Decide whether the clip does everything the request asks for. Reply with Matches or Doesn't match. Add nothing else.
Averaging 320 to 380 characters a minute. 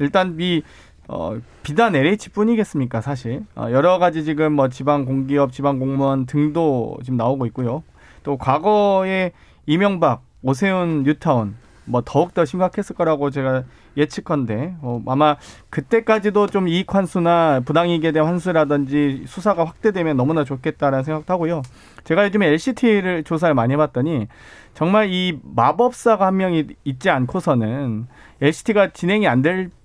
Matches